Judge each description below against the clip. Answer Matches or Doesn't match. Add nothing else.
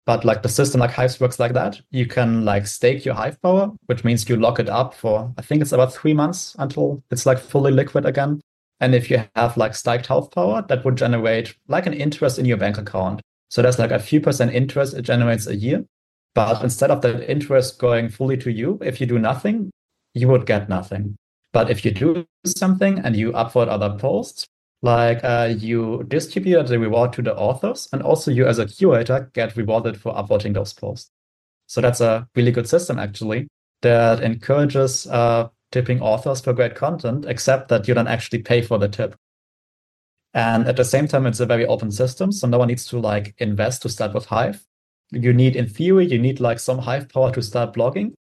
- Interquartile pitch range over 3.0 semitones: Doesn't match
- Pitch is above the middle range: Doesn't match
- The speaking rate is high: Matches